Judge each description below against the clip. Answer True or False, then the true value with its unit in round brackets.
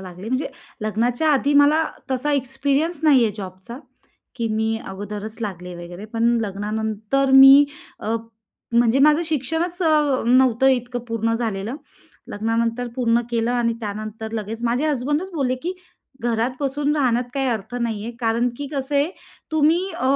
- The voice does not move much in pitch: False (4.2 semitones)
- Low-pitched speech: False (240 Hz)